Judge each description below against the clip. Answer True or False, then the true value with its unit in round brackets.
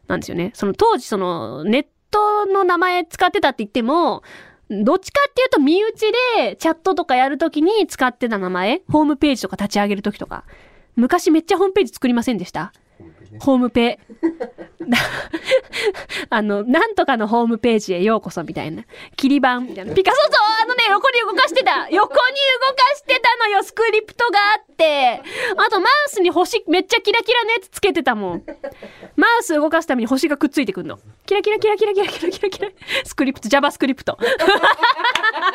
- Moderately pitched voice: False (325 Hz)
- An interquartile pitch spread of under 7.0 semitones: False (8.7 semitones)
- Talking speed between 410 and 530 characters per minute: False (390 characters per minute)